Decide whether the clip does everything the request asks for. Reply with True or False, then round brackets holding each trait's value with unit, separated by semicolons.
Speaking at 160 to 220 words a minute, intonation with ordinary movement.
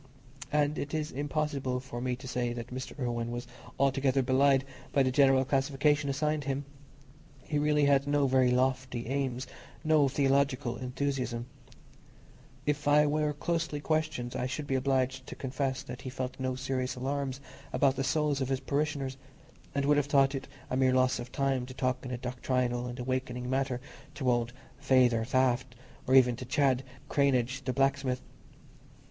False (170 wpm; 1.9 semitones)